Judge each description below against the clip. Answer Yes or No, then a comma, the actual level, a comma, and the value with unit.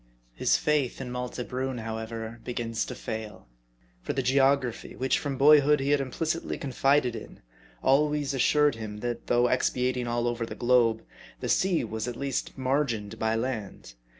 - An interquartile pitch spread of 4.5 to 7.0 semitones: No, average, 3.2 semitones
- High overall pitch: No, low, 125 Hz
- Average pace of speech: Yes, average, 160 wpm